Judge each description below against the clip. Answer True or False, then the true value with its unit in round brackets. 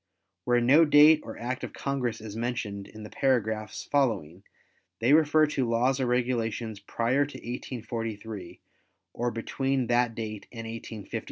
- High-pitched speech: False (120 Hz)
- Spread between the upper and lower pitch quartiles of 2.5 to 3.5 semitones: True (3.0 semitones)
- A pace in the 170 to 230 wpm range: False (150 wpm)